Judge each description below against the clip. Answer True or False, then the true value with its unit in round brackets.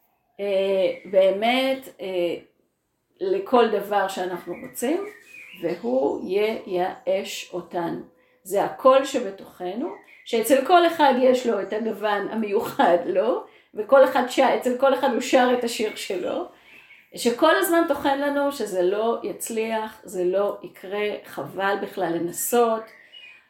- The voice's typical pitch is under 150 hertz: False (225 Hz)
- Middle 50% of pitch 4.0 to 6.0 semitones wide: True (5.6 semitones)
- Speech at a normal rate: True (110 wpm)